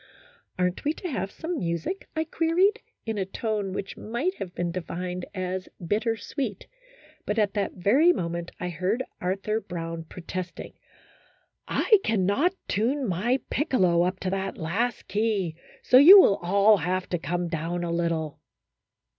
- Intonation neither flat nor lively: Yes, average, 5.0 semitones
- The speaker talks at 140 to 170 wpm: Yes, average, 160 wpm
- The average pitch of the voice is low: No, high, 195 Hz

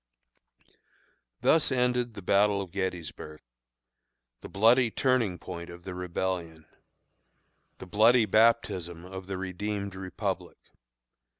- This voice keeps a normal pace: No, slow, 105 wpm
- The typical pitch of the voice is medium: No, very low, 95 Hz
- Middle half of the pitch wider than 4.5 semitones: No, average, 3.9 semitones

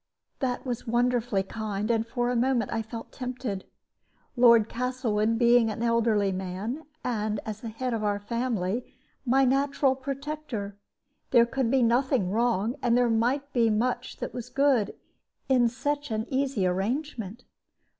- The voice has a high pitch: Yes, high, 235 Hz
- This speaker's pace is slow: No, average, 150 wpm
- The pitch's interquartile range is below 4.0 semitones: Yes, average, 2.9 semitones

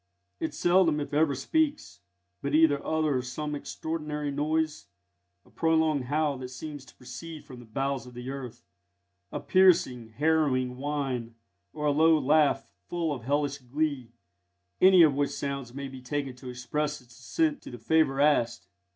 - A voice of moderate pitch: Yes, medium, 145 Hz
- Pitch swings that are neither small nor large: Yes, average, 3.4 semitones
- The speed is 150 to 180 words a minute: Yes, average, 160 wpm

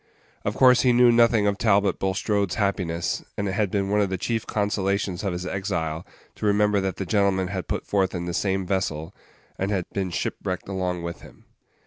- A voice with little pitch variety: Yes, narrow, 2.0 semitones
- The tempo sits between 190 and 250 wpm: Yes, average, 200 wpm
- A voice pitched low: Yes, very low, 95 Hz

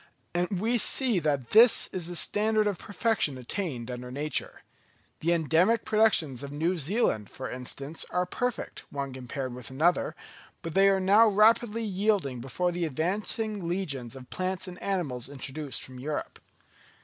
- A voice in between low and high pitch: Yes, medium, 175 Hz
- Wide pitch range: Yes, wide, 6.9 semitones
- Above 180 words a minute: No, average, 155 wpm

